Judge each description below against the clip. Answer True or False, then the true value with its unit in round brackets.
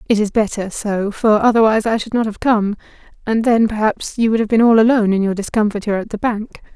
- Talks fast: True (230 wpm)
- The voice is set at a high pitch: True (215 Hz)